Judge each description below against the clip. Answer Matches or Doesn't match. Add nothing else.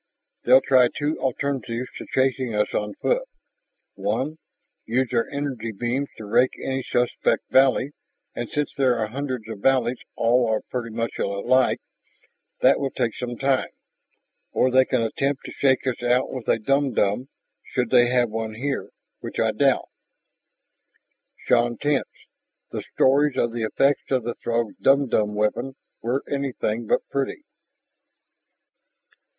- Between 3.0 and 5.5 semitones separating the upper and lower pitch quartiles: Doesn't match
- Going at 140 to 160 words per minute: Matches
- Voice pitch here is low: Matches